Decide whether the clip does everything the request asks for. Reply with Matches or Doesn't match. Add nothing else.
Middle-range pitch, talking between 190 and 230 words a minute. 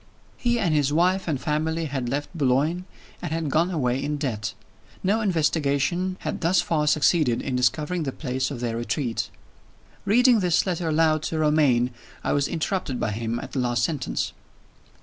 Doesn't match